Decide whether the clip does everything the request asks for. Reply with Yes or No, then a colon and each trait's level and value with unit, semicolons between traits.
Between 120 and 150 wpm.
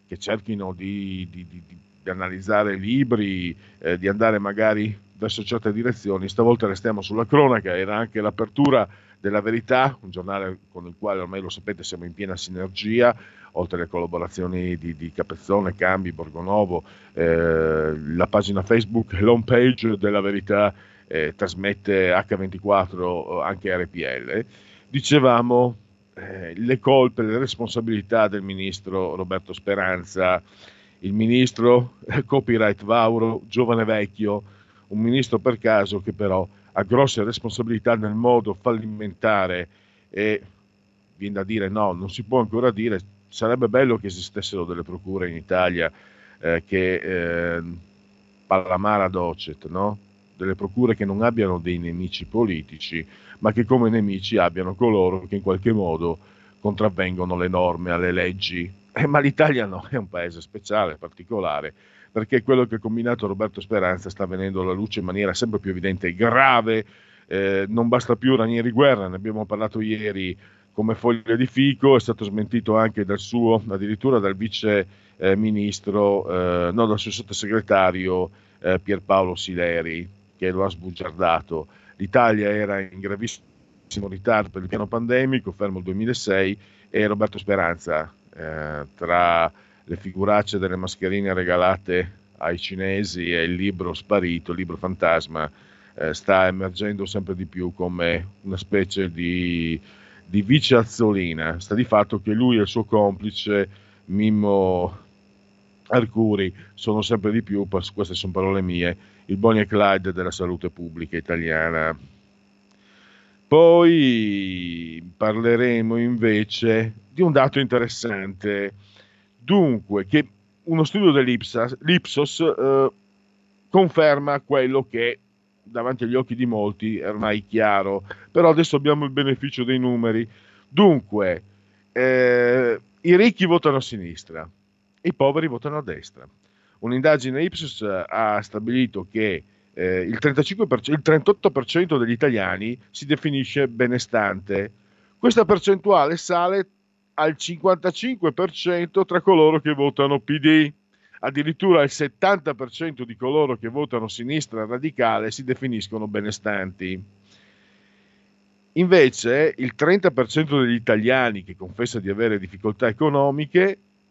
Yes: average, 130 wpm